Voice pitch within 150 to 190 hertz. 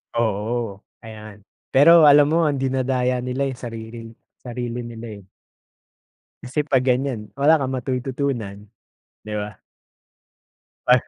No: low, 125 Hz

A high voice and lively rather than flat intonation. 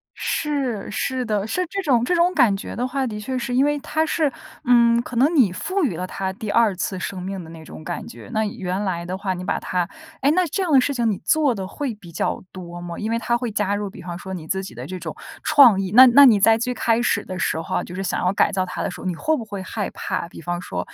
Yes: high, 215 Hz; wide, 5.7 semitones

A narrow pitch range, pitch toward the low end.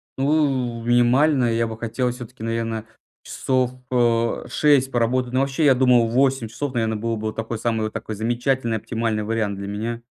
Yes: narrow, 2.3 semitones; low, 120 Hz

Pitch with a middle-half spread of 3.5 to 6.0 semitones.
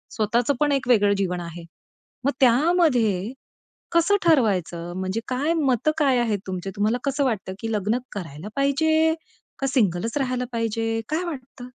Yes: wide, 5.6 semitones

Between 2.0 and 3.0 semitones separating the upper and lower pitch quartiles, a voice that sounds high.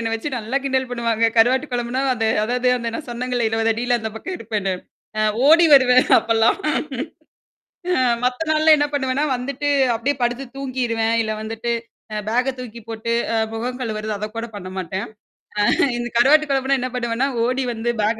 Yes: narrow, 2.6 semitones; high, 240 Hz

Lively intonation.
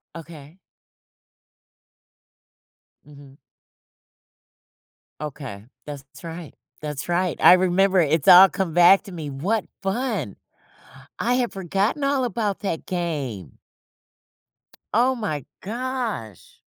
Yes: wide, 5.8 semitones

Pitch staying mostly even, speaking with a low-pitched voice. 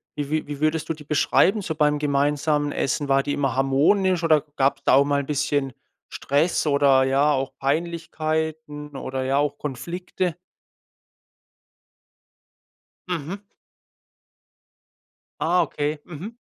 No: narrow, 2.3 semitones; medium, 150 Hz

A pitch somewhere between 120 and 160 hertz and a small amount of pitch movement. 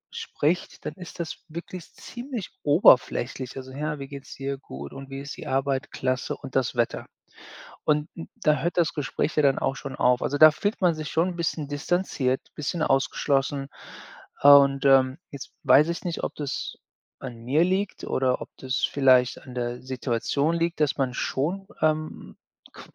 No: medium, 140 Hz; average, 3.2 semitones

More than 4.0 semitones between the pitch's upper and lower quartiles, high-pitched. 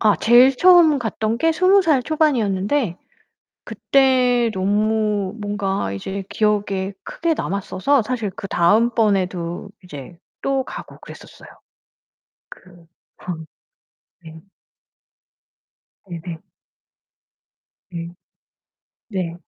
Yes: wide, 5.5 semitones; high, 210 Hz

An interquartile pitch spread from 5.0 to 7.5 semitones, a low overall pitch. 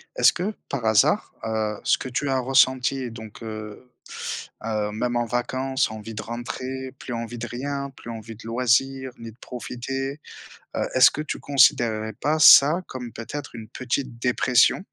No: average, 2.8 semitones; low, 125 Hz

